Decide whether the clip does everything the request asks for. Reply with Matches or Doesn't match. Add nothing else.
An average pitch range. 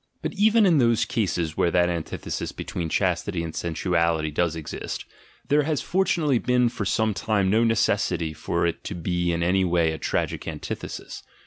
Doesn't match